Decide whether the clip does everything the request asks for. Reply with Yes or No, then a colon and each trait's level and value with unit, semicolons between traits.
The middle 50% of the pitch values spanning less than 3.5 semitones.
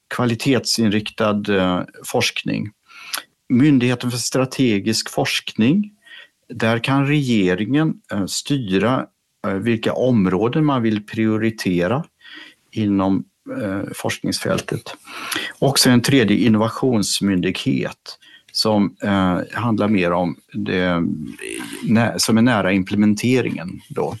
No: average, 4.2 semitones